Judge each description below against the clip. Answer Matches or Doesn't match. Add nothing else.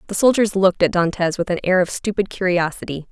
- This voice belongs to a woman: Matches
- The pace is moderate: Doesn't match